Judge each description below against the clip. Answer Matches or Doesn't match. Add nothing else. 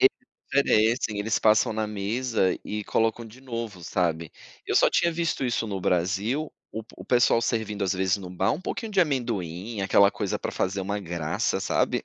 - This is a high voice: Doesn't match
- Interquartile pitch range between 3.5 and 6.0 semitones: Matches